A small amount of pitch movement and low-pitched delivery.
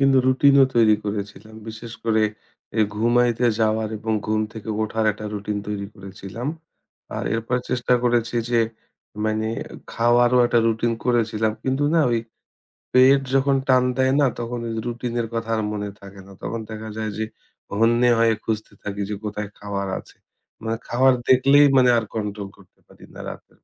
Yes: narrow, 2.3 semitones; low, 115 Hz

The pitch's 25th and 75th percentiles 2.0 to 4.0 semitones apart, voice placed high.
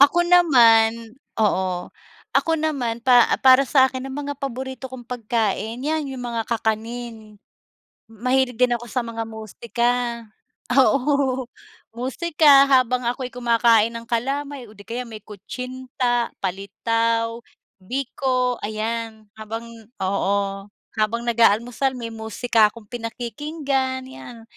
Yes: narrow, 2.6 semitones; high, 240 Hz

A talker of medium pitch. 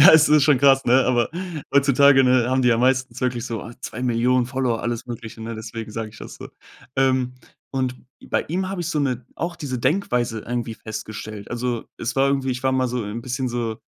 No: low, 125 Hz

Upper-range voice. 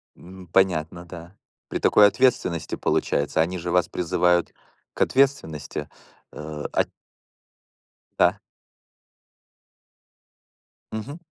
No: very low, 90 Hz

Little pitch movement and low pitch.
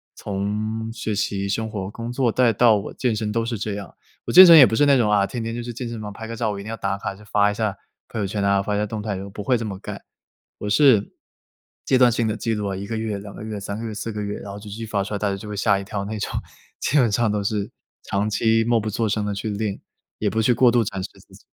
Yes: narrow, 2.0 semitones; low, 105 Hz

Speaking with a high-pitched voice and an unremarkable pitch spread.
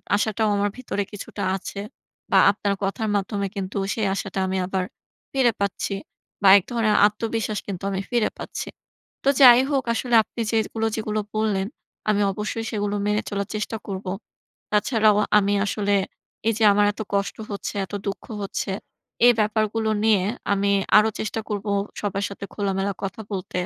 No: high, 205 Hz; narrow, 1.8 semitones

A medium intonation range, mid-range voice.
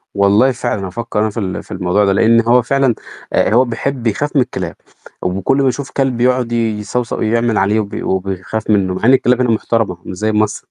No: average, 3.6 semitones; low, 110 Hz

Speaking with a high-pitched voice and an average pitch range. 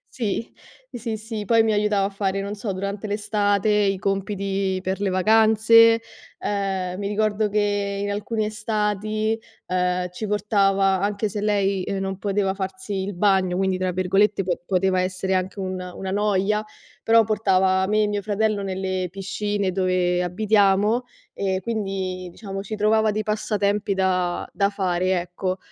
No: high, 200 Hz; narrow, 1.9 semitones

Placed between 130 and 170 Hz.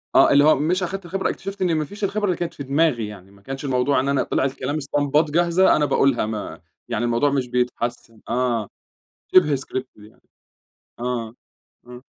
Yes: low, 135 Hz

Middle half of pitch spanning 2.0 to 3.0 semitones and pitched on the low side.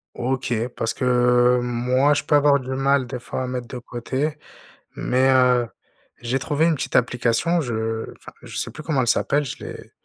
Yes: narrow, 2.6 semitones; low, 130 Hz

